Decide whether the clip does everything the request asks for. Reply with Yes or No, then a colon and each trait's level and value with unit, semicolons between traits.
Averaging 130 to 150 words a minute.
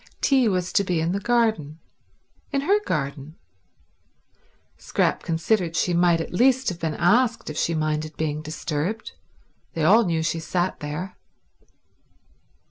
Yes: average, 140 wpm